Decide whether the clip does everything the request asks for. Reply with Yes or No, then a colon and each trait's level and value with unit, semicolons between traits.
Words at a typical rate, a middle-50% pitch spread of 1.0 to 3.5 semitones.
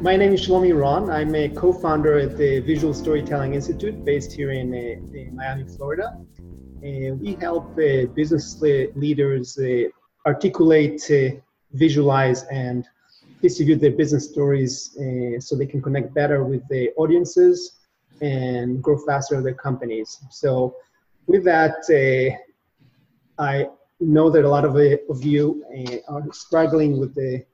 No: slow, 130 wpm; average, 2.7 semitones